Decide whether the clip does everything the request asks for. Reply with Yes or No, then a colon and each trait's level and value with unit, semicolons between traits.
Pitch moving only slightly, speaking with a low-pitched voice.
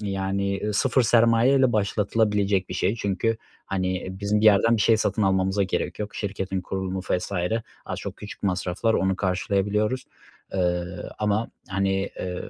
Yes: narrow, 2.0 semitones; low, 100 Hz